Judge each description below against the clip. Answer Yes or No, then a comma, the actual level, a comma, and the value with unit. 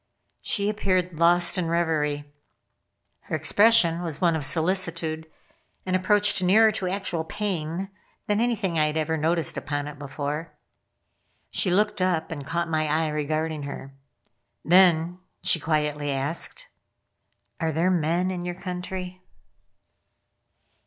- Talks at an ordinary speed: No, slow, 130 wpm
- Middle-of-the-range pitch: Yes, medium, 170 Hz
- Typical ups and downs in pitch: Yes, average, 3.0 semitones